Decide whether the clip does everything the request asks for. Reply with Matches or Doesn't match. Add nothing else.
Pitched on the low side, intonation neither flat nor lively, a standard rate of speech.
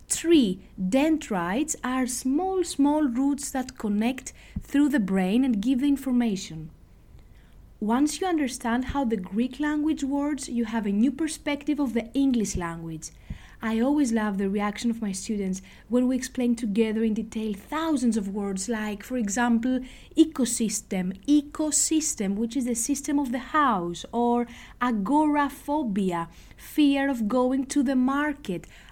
Doesn't match